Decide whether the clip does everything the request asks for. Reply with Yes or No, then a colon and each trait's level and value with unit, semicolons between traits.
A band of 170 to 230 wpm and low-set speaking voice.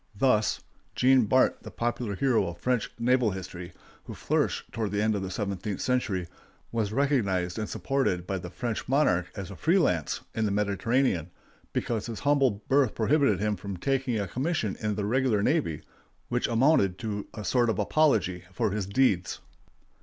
Yes: average, 175 wpm; low, 110 Hz